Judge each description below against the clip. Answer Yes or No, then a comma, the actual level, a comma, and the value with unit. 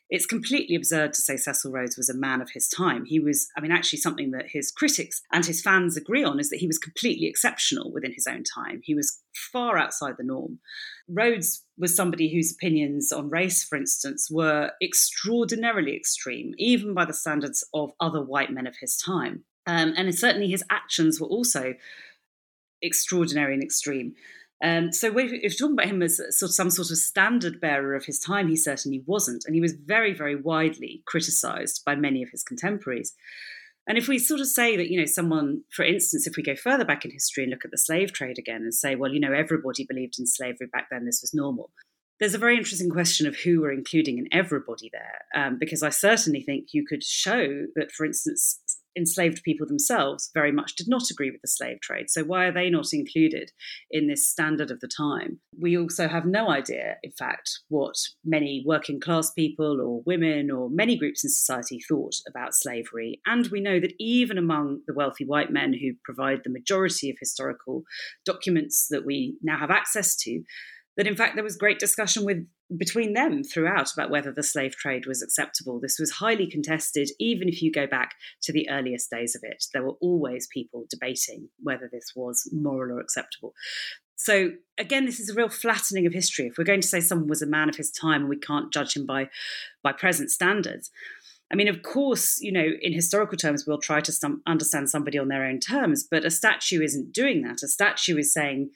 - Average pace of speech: No, fast, 210 wpm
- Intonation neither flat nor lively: No, wide, 5.9 semitones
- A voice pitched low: No, medium, 165 Hz